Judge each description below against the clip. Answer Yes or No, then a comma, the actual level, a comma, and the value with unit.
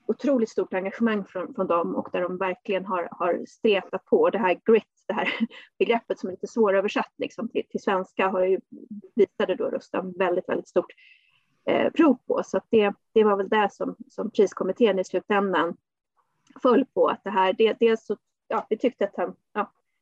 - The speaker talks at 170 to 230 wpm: Yes, average, 190 wpm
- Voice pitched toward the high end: Yes, high, 205 Hz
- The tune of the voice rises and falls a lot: No, average, 3.4 semitones